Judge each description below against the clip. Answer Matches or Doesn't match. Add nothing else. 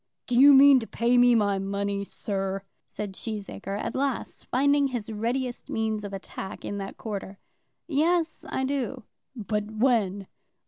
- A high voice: Matches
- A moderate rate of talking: Matches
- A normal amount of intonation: Matches